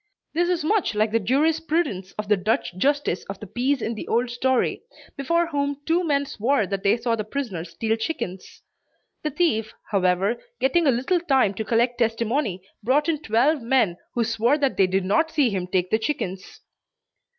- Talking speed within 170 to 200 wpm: Yes, average, 185 wpm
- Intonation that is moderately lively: No, wide, 6.0 semitones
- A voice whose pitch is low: No, high, 235 Hz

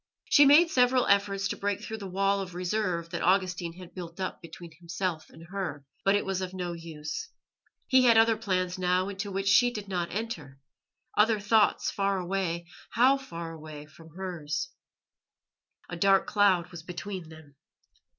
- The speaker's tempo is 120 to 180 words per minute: Yes, average, 170 wpm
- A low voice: No, medium, 185 Hz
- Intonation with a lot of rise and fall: No, average, 3.2 semitones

